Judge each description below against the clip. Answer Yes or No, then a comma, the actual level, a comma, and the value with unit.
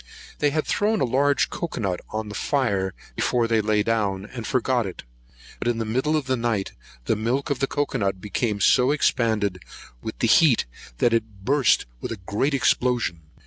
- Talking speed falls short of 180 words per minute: No, average, 185 wpm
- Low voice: Yes, low, 115 Hz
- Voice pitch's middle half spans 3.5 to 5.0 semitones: Yes, average, 4.2 semitones